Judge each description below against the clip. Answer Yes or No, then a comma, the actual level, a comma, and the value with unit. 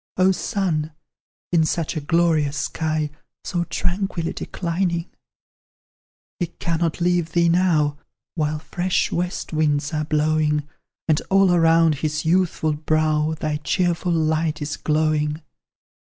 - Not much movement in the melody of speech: Yes, narrow, 2.1 semitones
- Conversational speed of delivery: No, slow, 120 wpm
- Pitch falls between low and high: Yes, medium, 160 Hz